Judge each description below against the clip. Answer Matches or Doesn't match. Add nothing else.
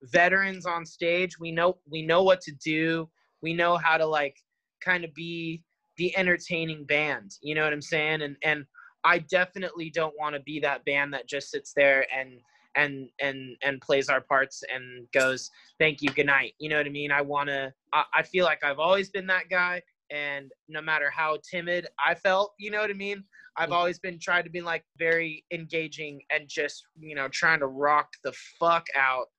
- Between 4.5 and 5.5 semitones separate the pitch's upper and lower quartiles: Doesn't match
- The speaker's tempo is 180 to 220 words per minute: Matches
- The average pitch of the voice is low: Doesn't match